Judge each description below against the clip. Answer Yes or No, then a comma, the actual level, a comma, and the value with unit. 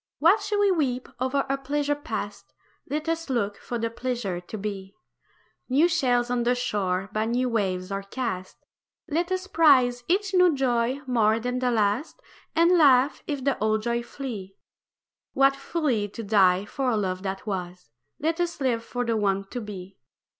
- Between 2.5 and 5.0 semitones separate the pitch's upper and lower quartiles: No, wide, 5.6 semitones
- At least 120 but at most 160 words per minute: No, average, 175 wpm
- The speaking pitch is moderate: No, high, 245 Hz